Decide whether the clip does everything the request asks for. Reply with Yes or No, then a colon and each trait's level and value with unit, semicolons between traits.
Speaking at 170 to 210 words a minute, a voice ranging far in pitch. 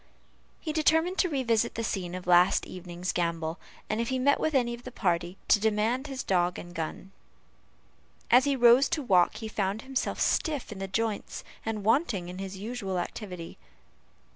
Yes: average, 185 wpm; wide, 5.7 semitones